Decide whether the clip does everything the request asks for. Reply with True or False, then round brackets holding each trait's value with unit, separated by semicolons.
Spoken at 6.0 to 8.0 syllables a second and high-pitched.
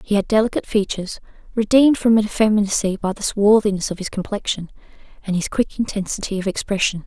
True (6.4 syllables/s; 205 Hz)